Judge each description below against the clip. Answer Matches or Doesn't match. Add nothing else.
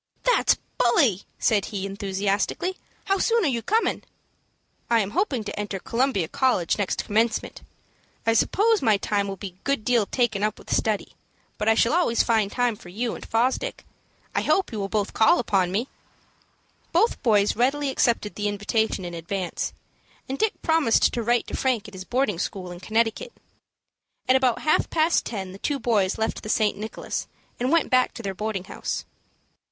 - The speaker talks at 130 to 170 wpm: Doesn't match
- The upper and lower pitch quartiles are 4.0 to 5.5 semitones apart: Matches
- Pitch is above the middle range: Matches